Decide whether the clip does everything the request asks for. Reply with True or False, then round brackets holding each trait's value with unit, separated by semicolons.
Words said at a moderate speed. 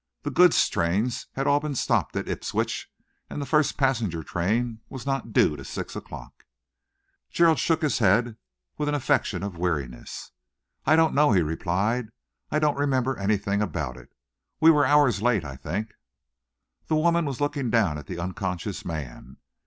True (170 wpm)